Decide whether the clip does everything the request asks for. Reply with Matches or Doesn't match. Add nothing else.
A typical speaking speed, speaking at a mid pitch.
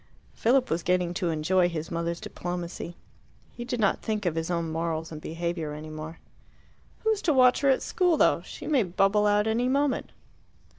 Matches